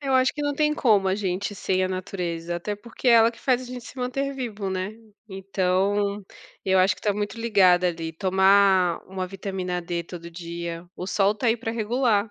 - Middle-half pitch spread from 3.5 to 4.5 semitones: Yes, average, 3.8 semitones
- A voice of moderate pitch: No, high, 195 Hz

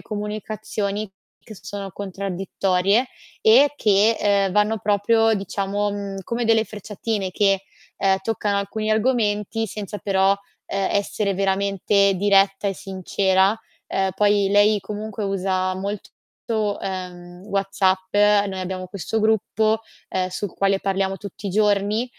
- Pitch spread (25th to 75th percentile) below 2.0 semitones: Yes, narrow, 1.6 semitones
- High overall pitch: Yes, high, 200 Hz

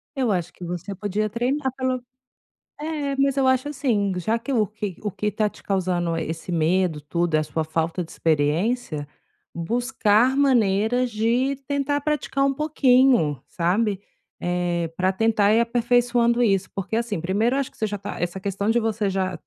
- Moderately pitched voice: No, high, 210 Hz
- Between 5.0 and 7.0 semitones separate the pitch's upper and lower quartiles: Yes, wide, 5.6 semitones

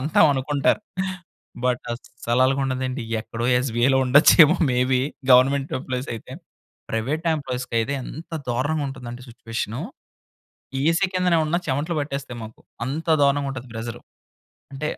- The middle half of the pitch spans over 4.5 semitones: No, average, 2.8 semitones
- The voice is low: Yes, low, 130 Hz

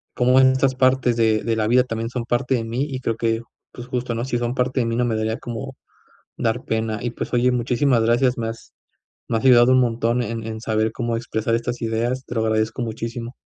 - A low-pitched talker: Yes, low, 120 Hz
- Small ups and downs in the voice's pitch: Yes, narrow, 1.8 semitones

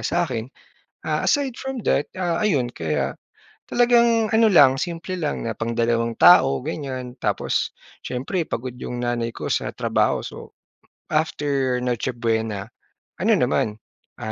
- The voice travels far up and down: Yes, wide, 7.0 semitones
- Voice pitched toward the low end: Yes, low, 130 Hz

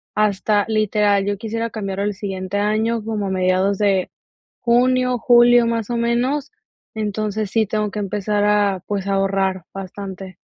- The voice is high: Yes, high, 210 Hz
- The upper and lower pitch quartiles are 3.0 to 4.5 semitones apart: No, narrow, 2.5 semitones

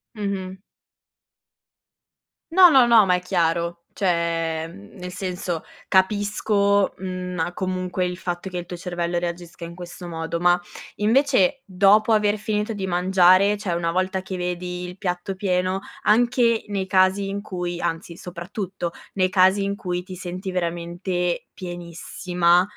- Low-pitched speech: No, medium, 185 Hz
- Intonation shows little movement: Yes, narrow, 2.2 semitones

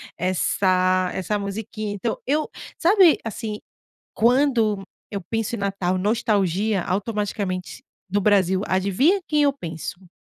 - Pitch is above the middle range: Yes, high, 205 Hz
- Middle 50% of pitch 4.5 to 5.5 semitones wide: No, average, 3.4 semitones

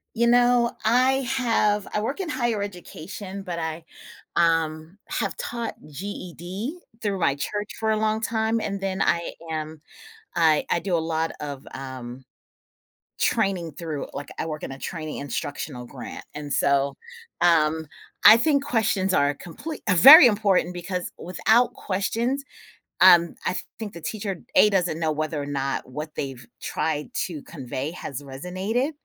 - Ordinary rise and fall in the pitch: No, wide, 6.0 semitones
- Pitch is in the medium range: Yes, medium, 175 Hz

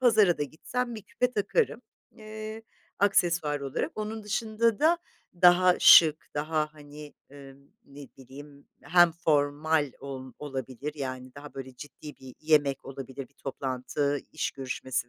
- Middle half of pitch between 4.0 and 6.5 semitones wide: Yes, average, 5.1 semitones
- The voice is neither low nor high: Yes, medium, 150 Hz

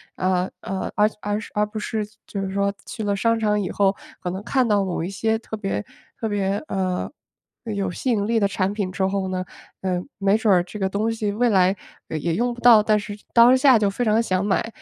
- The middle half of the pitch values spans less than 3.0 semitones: Yes, narrow, 2.5 semitones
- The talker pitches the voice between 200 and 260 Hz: Yes, high, 205 Hz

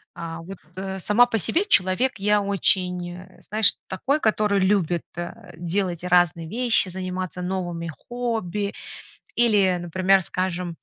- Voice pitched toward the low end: No, medium, 185 Hz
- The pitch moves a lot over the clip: No, average, 2.8 semitones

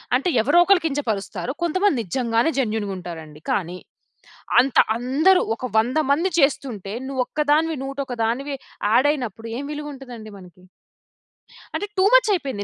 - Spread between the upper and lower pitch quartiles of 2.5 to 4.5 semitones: No, average, 5.3 semitones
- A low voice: No, very high, 260 Hz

